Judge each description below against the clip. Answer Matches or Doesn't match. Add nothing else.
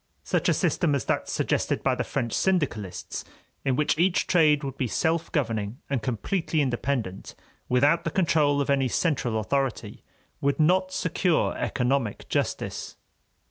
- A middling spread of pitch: Matches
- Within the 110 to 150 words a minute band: Matches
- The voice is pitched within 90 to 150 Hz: Matches